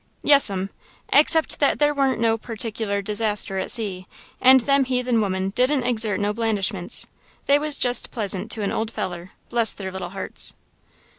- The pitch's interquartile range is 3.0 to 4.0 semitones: No, average, 4.5 semitones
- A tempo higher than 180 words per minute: No, average, 160 wpm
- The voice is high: Yes, high, 225 Hz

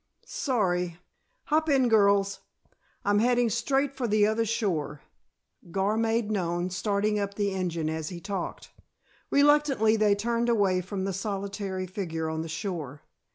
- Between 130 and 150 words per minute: Yes, average, 145 wpm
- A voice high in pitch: Yes, high, 200 Hz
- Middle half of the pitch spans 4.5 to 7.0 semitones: No, average, 3.8 semitones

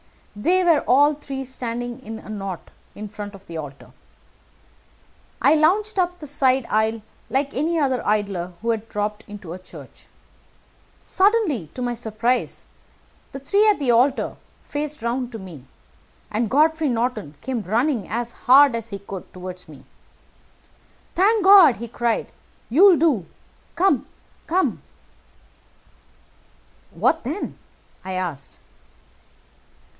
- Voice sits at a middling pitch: No, high, 245 Hz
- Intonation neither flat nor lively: No, wide, 6.3 semitones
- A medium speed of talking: No, slow, 130 wpm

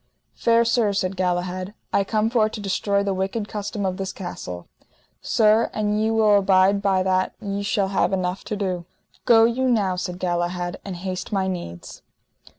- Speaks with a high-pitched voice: Yes, high, 195 Hz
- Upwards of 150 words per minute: Yes, average, 175 wpm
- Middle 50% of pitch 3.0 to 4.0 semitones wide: No, narrow, 2.5 semitones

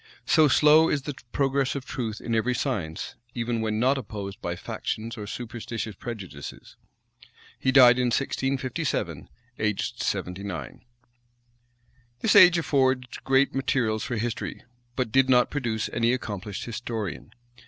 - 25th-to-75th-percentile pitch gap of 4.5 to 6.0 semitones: No, average, 3.6 semitones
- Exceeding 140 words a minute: No, slow, 135 wpm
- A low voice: Yes, low, 120 Hz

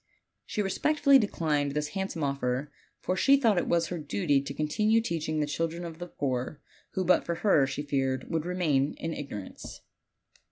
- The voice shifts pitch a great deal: No, average, 4.5 semitones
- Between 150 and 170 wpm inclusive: No, average, 190 wpm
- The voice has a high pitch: No, medium, 160 Hz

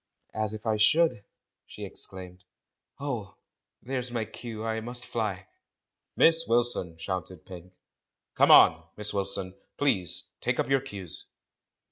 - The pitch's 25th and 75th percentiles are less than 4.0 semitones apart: No, average, 4.6 semitones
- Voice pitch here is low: Yes, low, 110 Hz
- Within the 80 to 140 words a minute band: Yes, slow, 135 wpm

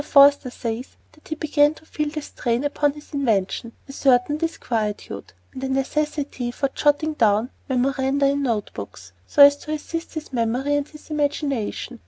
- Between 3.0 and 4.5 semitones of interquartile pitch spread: Yes, average, 3.3 semitones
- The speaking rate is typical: Yes, average, 170 wpm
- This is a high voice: Yes, very high, 280 Hz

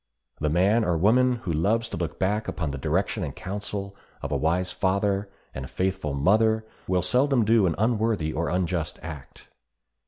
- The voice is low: Yes, very low, 95 Hz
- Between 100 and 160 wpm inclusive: No, average, 175 wpm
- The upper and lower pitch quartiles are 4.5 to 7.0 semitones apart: Yes, average, 4.8 semitones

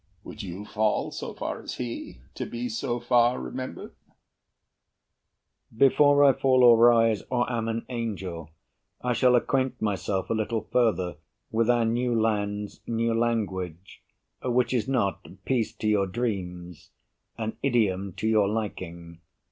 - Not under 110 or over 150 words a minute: Yes, average, 145 wpm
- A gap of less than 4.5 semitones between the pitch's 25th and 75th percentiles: Yes, average, 3.3 semitones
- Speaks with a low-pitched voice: Yes, low, 115 Hz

